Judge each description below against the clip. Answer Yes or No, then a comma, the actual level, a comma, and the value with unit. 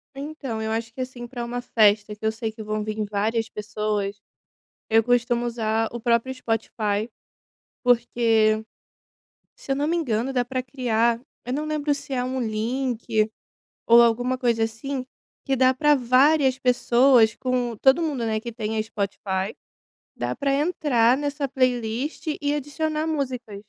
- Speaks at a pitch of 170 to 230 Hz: No, high, 240 Hz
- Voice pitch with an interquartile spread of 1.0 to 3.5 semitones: Yes, average, 3.2 semitones